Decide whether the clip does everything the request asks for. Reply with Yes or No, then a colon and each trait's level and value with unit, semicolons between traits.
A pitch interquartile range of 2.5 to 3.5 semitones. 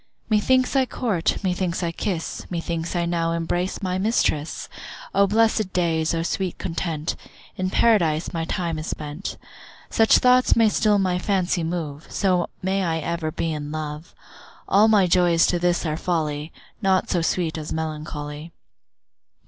Yes: average, 3.0 semitones